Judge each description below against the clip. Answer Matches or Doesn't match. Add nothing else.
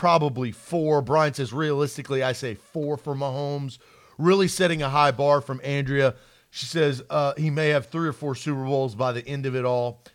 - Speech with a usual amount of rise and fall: Doesn't match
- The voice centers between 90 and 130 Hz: Doesn't match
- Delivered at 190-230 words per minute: Matches